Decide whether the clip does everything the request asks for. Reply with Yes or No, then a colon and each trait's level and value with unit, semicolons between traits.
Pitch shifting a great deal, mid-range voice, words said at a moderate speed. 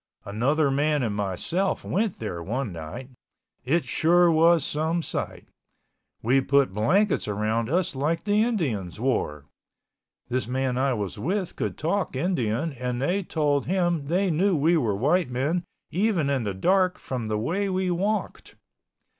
Yes: wide, 6.5 semitones; medium, 145 Hz; average, 155 wpm